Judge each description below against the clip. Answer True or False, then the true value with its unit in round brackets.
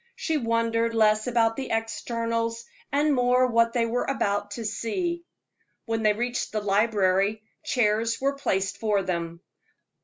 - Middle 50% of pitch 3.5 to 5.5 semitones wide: False (2.4 semitones)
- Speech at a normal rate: True (145 wpm)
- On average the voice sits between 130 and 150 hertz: False (230 Hz)